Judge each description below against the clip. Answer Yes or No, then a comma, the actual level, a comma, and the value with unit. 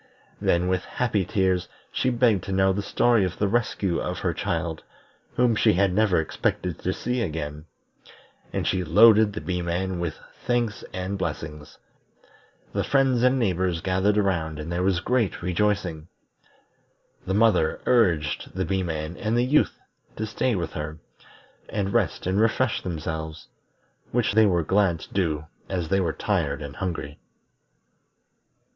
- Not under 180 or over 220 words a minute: No, average, 155 wpm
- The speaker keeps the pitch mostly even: No, average, 4.3 semitones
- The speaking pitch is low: Yes, very low, 95 Hz